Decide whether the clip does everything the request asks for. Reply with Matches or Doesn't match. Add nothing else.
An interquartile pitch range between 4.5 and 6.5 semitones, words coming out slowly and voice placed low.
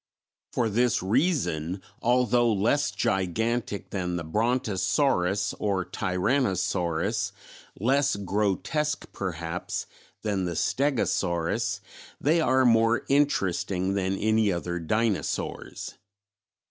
Matches